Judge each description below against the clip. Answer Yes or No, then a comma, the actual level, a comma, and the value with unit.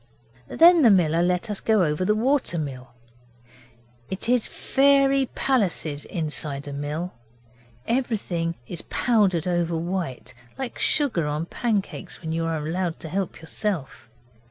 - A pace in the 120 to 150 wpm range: Yes, average, 140 wpm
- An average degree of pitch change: No, wide, 5.8 semitones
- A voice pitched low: No, medium, 175 Hz